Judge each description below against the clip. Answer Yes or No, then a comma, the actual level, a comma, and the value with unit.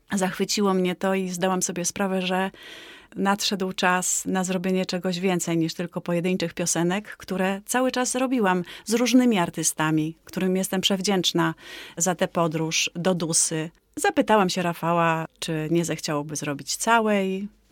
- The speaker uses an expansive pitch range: No, narrow, 2.6 semitones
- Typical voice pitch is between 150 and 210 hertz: Yes, medium, 185 Hz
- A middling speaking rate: Yes, average, 140 wpm